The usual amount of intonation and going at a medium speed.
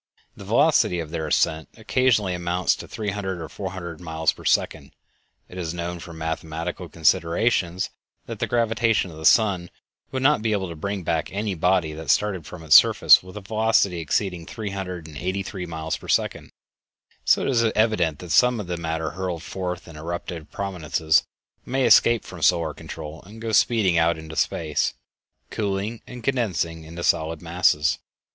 Yes: average, 4.2 semitones; average, 180 wpm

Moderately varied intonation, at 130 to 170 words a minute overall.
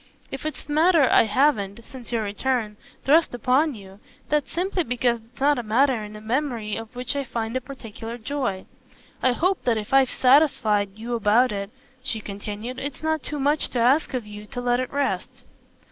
No: average, 4.3 semitones; average, 195 wpm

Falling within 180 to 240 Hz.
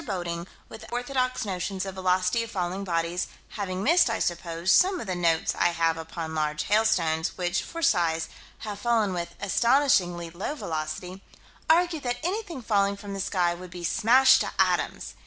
Yes: high, 190 Hz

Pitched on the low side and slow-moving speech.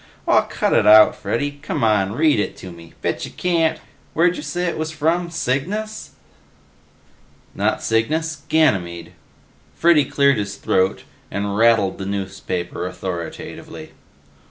Yes: low, 120 Hz; slow, 130 wpm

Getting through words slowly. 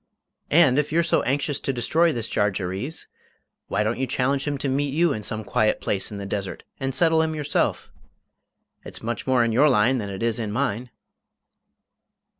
No: average, 190 wpm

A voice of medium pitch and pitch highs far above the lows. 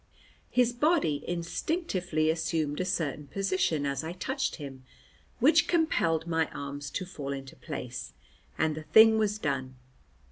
Yes: medium, 165 Hz; wide, 6.8 semitones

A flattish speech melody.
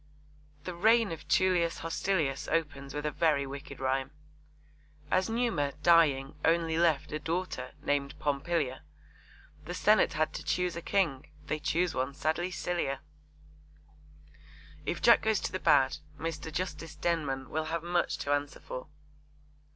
No: average, 3.6 semitones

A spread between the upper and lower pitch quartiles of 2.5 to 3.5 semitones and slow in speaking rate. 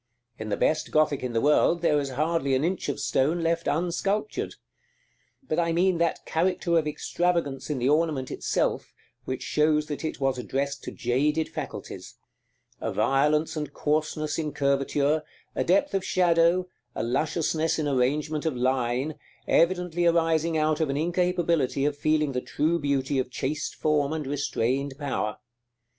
No: average, 3.2 semitones; average, 160 wpm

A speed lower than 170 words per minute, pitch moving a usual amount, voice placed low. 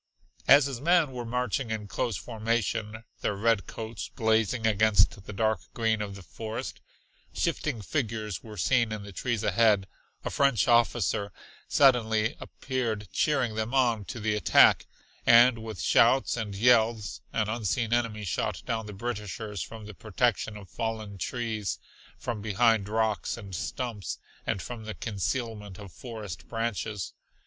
No: average, 150 wpm; narrow, 2.2 semitones; low, 110 Hz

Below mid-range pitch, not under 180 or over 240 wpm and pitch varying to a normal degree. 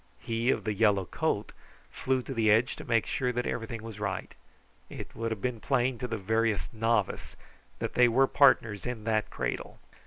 No: low, 115 Hz; average, 190 wpm; narrow, 2.3 semitones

